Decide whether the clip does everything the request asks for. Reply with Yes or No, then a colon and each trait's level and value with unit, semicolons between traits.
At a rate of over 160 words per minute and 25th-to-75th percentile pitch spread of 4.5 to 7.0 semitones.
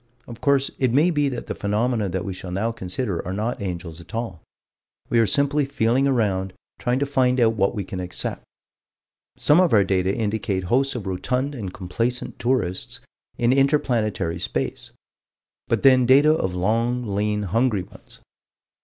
Yes: average, 170 wpm; average, 5.2 semitones